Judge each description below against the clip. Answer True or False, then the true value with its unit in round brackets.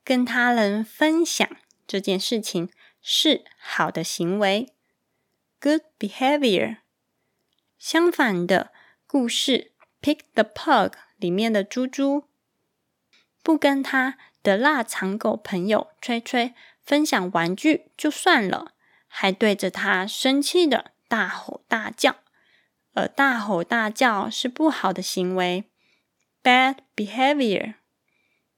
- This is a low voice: False (240 Hz)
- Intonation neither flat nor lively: False (6.4 semitones)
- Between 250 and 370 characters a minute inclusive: False (205 characters per minute)